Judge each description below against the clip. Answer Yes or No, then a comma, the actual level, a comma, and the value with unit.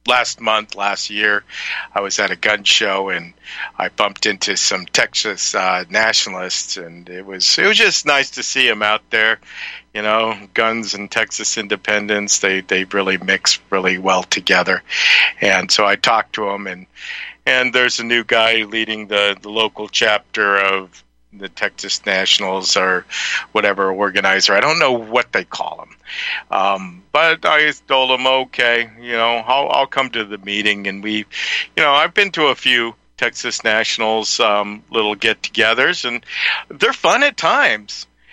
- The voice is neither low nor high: No, low, 105 Hz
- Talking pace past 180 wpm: No, average, 170 wpm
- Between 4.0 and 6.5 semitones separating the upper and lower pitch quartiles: No, average, 2.8 semitones